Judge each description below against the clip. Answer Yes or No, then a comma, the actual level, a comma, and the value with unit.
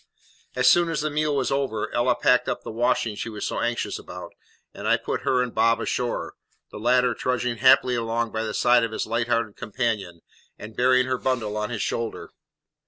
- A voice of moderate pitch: No, low, 120 Hz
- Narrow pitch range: Yes, narrow, 2.1 semitones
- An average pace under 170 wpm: No, fast, 205 wpm